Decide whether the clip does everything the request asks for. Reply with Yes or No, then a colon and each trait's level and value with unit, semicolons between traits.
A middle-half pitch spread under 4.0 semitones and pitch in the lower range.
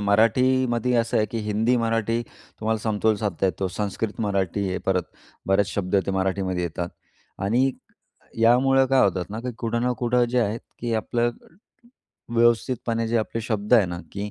Yes: average, 2.9 semitones; low, 110 Hz